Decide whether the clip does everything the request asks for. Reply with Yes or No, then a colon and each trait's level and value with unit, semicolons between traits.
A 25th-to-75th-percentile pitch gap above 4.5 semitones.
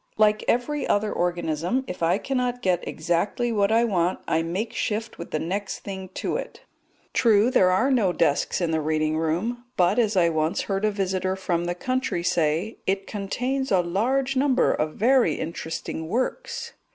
Yes: wide, 5.6 semitones